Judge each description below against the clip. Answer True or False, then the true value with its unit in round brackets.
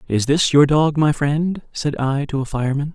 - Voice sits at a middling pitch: True (145 Hz)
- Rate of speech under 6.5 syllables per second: True (4.8 syllables/s)